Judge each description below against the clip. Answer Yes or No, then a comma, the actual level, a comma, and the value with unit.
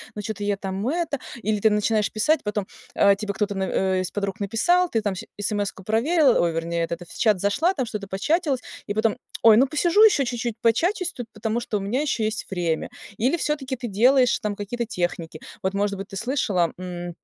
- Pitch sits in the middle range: No, high, 215 Hz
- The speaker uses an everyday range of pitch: Yes, average, 4.6 semitones